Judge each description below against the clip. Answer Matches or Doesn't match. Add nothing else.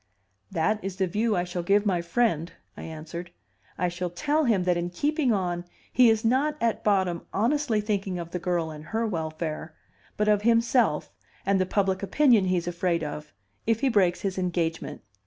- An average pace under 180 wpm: Doesn't match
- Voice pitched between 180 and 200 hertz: Matches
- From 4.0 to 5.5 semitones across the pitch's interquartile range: Matches